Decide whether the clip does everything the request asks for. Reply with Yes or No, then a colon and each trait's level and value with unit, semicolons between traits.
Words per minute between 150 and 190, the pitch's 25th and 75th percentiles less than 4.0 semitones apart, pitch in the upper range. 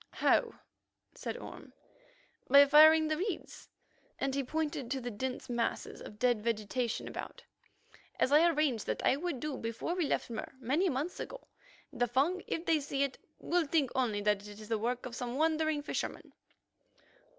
No: average, 165 wpm; average, 4.7 semitones; very high, 275 Hz